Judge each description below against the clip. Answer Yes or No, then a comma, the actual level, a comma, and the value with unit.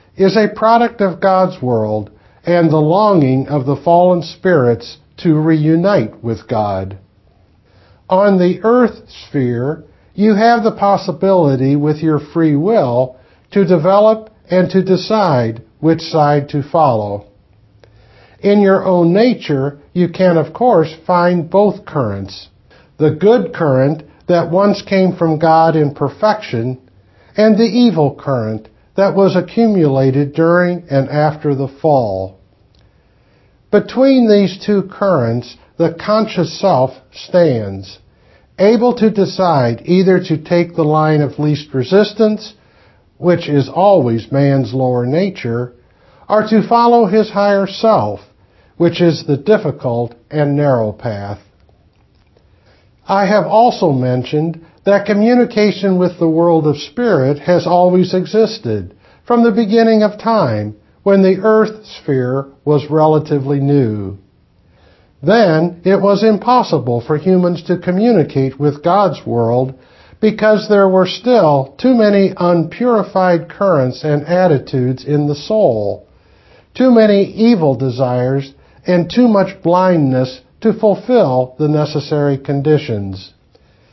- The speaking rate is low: Yes, slow, 125 wpm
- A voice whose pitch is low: No, medium, 160 Hz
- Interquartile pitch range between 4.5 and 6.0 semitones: No, wide, 7.3 semitones